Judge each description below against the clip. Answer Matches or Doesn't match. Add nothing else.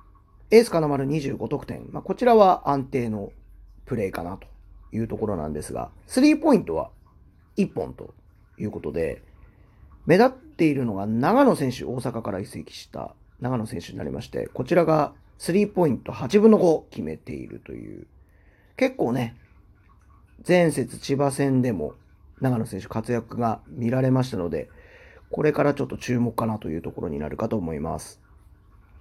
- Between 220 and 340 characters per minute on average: Matches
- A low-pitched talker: Matches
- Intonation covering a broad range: Matches